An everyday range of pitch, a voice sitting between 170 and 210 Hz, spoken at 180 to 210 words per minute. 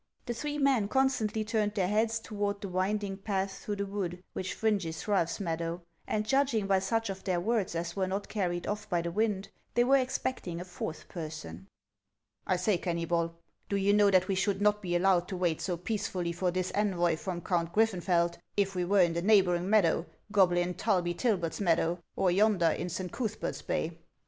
Yes: average, 3.2 semitones; high, 190 Hz; average, 195 wpm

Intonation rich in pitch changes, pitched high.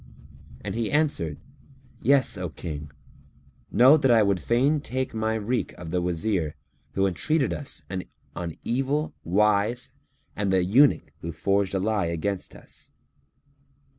No: wide, 6.0 semitones; low, 105 Hz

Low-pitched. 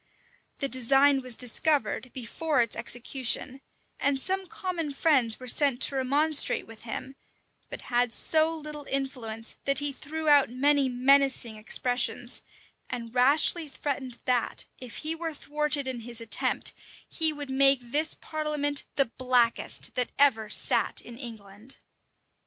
No: very high, 270 Hz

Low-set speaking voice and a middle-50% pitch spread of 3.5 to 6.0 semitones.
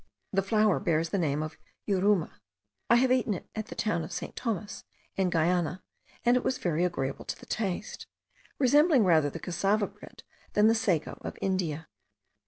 No: high, 190 Hz; average, 4.5 semitones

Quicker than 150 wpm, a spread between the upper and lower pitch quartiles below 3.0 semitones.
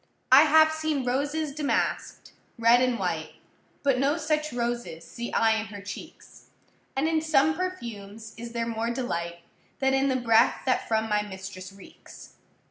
No: average, 160 wpm; average, 4.8 semitones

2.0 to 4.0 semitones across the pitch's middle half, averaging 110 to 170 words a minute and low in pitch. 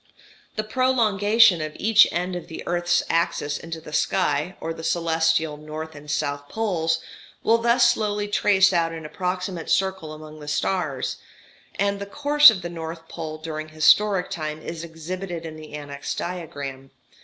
No: average, 3.7 semitones; average, 160 wpm; medium, 165 Hz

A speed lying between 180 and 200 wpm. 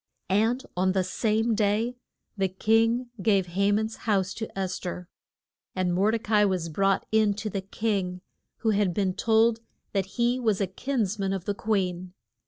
Yes: average, 185 wpm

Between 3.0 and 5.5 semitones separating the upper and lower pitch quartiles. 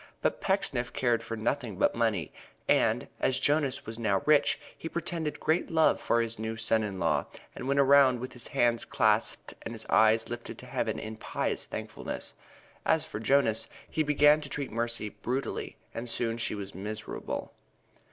Yes: average, 4.1 semitones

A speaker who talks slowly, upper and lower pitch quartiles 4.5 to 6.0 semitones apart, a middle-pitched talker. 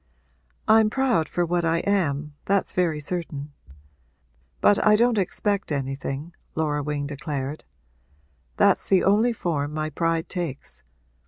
Yes: slow, 130 wpm; average, 5.2 semitones; medium, 165 Hz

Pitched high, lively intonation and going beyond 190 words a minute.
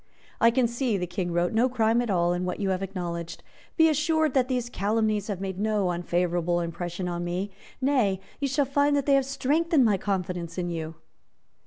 Yes: high, 200 Hz; wide, 6.5 semitones; average, 200 wpm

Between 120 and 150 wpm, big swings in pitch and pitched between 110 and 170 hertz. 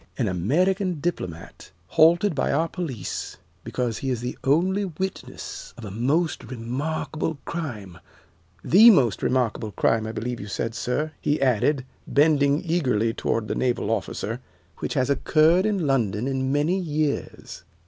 Yes: average, 145 wpm; wide, 6.0 semitones; low, 135 Hz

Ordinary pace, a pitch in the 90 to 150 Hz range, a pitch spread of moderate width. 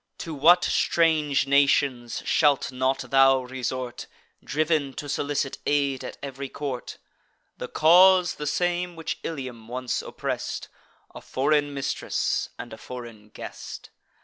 No: slow, 125 wpm; medium, 140 Hz; average, 3.0 semitones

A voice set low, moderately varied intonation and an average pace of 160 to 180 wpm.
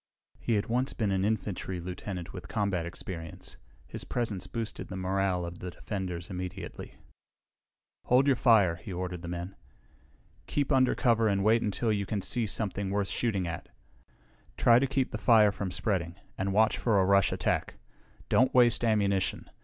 Yes: low, 100 Hz; average, 3.7 semitones; average, 170 wpm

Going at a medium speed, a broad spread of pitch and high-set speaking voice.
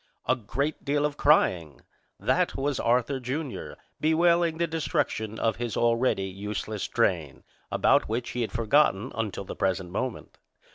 No: average, 145 wpm; wide, 5.8 semitones; low, 120 Hz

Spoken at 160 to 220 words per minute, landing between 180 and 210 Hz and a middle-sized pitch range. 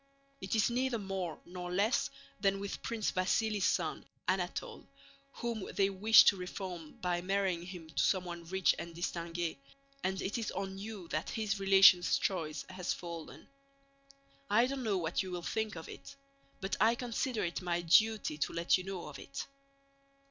Yes: average, 170 wpm; high, 190 Hz; average, 3.3 semitones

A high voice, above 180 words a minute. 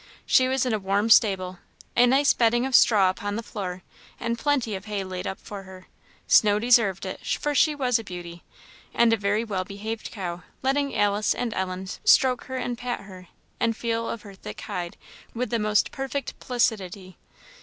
Yes: high, 215 Hz; average, 190 wpm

